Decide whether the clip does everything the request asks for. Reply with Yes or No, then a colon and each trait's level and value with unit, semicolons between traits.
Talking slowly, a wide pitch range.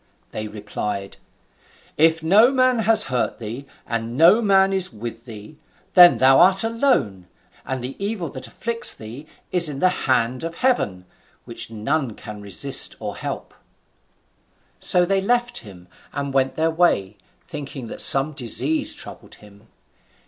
No: average, 150 wpm; wide, 8.4 semitones